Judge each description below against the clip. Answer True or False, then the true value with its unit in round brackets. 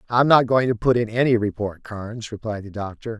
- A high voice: False (115 Hz)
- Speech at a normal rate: False (225 wpm)